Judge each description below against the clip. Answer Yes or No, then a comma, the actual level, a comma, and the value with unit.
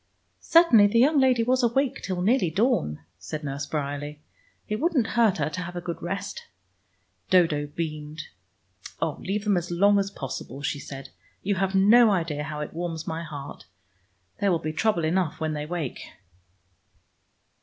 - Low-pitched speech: No, medium, 175 Hz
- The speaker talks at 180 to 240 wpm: No, average, 165 wpm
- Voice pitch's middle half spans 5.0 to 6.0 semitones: Yes, wide, 5.5 semitones